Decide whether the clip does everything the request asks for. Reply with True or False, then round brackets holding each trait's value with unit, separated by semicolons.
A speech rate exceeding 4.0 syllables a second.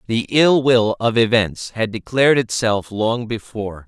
True (4.4 syllables/s)